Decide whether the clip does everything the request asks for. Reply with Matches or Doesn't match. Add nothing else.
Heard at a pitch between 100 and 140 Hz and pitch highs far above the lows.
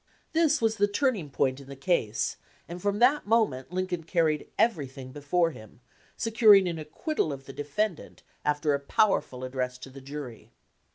Doesn't match